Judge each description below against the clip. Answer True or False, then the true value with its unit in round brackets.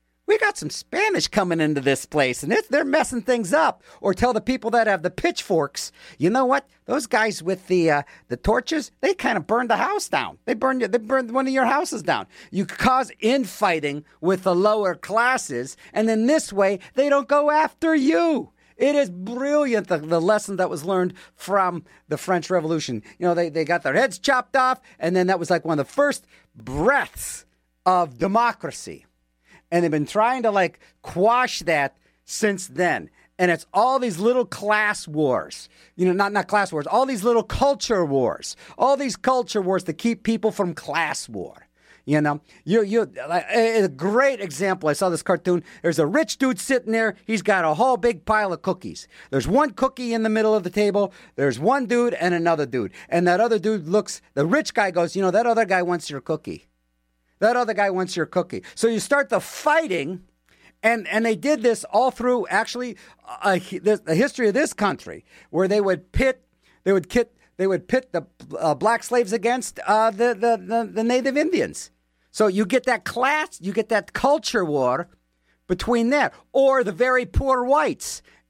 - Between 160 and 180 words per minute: False (195 wpm)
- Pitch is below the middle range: False (210 Hz)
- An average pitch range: False (6.0 semitones)